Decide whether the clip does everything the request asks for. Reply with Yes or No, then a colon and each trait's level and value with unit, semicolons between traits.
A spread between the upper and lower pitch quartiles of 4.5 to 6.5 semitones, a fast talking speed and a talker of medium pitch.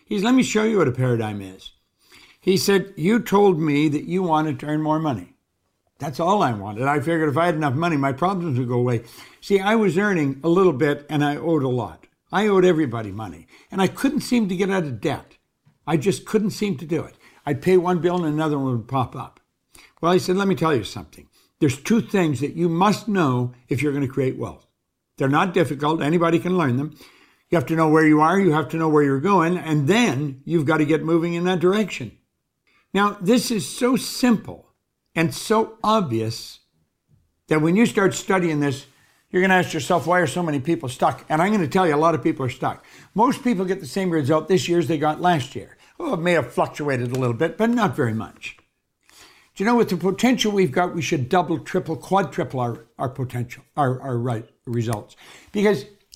Yes: average, 5.2 semitones; fast, 230 wpm; medium, 165 Hz